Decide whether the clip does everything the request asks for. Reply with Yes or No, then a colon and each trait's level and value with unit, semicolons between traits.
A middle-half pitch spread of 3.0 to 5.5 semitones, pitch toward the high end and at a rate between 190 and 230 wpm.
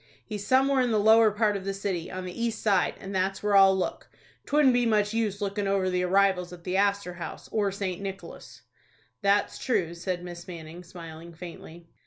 No: narrow, 2.5 semitones; high, 195 Hz; average, 200 wpm